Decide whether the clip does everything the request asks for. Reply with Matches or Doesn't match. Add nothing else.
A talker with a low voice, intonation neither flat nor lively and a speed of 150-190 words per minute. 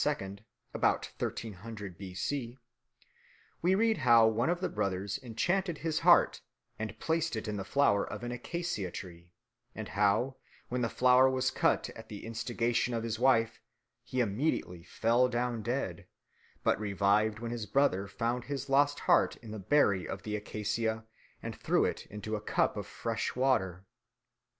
Matches